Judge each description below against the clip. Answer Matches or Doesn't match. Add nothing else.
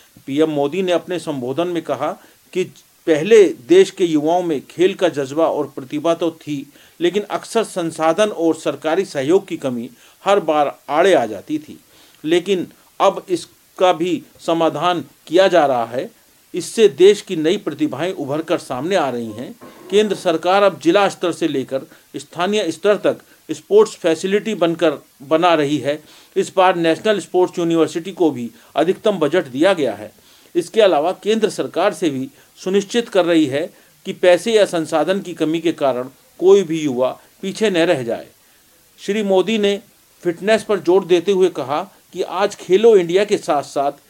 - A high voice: Doesn't match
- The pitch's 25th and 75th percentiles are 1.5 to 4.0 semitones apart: Doesn't match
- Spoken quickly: Doesn't match